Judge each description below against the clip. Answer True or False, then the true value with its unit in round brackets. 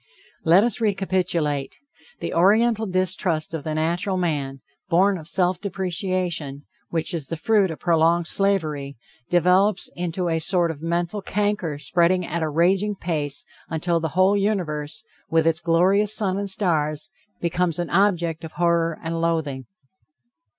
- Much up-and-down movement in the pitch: False (2.9 semitones)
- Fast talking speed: False (145 wpm)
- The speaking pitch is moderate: True (170 Hz)